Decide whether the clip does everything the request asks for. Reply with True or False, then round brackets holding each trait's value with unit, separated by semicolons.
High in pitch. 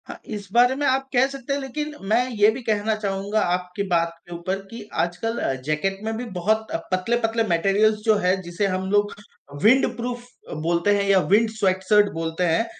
True (205 Hz)